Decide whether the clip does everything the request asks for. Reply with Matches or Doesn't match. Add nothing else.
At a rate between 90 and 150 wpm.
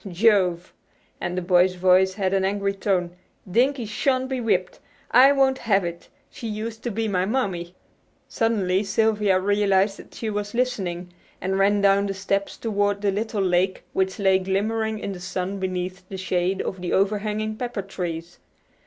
Doesn't match